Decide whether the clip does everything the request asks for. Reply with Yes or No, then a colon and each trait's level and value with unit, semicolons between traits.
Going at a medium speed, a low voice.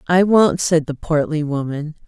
No: average, 175 wpm; medium, 160 Hz